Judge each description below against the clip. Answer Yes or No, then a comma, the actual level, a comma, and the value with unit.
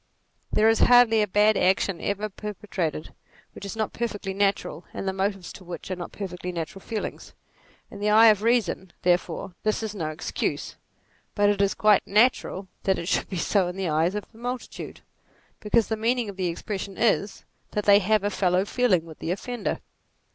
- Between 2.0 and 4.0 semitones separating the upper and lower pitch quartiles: Yes, average, 2.7 semitones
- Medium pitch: No, high, 200 Hz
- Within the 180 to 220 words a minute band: Yes, average, 200 wpm